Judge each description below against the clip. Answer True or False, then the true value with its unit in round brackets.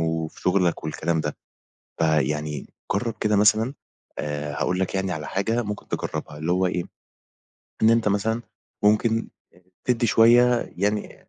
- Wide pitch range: True (5.8 semitones)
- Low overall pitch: True (95 Hz)